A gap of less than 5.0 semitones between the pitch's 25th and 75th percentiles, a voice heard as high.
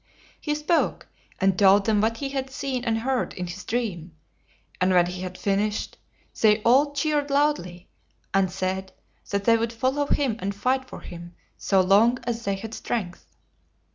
No: wide, 5.5 semitones; high, 220 Hz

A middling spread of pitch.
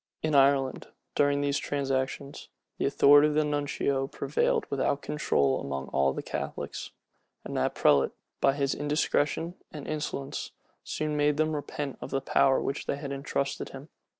No: narrow, 1.5 semitones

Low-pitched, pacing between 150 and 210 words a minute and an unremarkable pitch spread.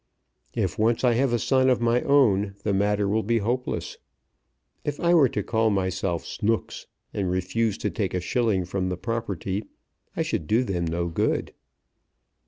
Yes: low, 105 Hz; average, 175 wpm; average, 3.9 semitones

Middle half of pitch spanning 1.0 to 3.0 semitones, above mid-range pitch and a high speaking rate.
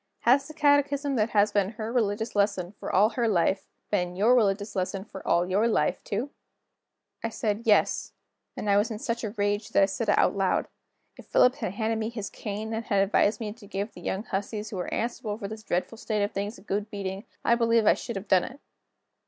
Yes: narrow, 2.5 semitones; high, 210 Hz; fast, 225 wpm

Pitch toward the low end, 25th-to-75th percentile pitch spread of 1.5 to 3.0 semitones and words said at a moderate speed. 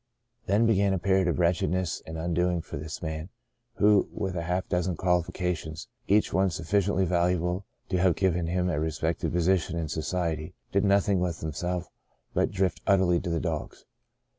Yes: very low, 90 Hz; narrow, 2.4 semitones; average, 165 wpm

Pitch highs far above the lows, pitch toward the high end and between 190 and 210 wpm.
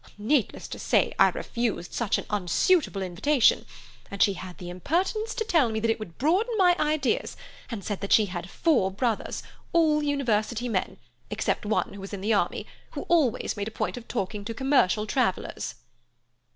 No: wide, 6.9 semitones; high, 225 Hz; average, 180 wpm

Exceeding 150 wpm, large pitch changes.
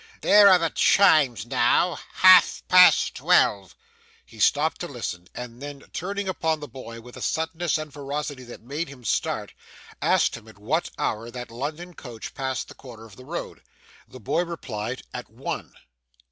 Yes: average, 165 wpm; wide, 5.8 semitones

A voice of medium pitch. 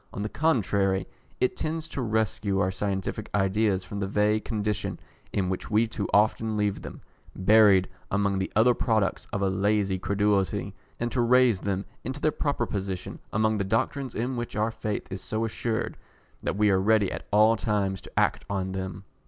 No: low, 105 Hz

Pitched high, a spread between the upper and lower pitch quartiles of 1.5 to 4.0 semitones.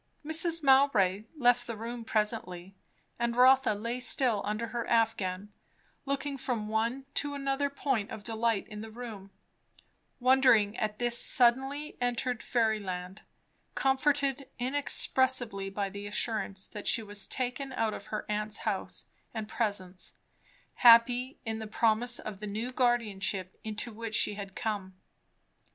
Yes: high, 225 Hz; average, 3.3 semitones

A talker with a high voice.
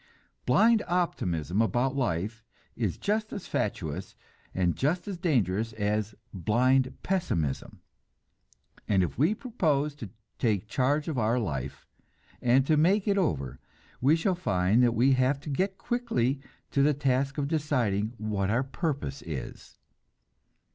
No: low, 130 Hz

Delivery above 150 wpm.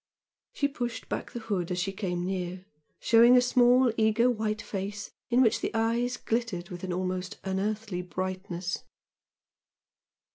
No: average, 145 wpm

